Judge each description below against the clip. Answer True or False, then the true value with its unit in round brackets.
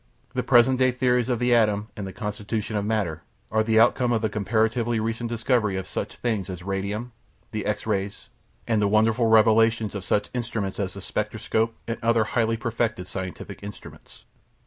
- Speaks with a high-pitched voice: False (110 Hz)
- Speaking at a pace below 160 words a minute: False (180 wpm)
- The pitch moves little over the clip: True (2.2 semitones)